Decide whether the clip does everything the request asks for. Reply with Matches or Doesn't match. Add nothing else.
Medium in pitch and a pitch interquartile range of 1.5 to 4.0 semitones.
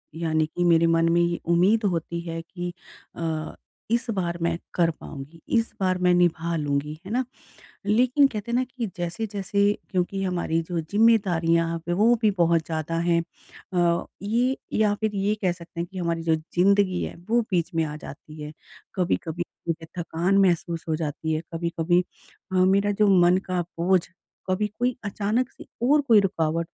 Matches